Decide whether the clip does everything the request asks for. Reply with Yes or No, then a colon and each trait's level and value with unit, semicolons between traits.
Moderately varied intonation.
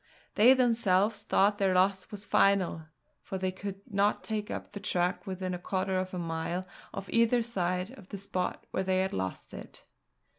No: narrow, 2.0 semitones